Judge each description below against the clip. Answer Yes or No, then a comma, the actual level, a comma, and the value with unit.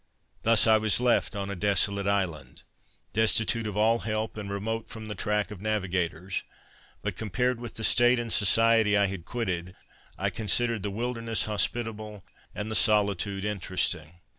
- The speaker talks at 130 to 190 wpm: Yes, average, 160 wpm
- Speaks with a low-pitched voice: Yes, low, 105 Hz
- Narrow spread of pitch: Yes, narrow, 2.3 semitones